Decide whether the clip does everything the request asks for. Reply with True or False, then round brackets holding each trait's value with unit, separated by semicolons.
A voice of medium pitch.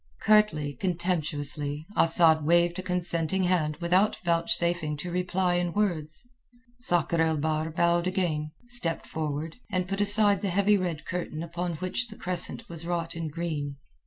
True (170 Hz)